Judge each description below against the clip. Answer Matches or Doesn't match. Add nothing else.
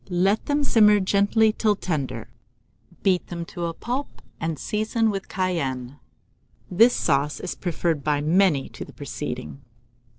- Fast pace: Doesn't match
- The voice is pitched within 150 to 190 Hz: Matches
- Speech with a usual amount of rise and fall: Doesn't match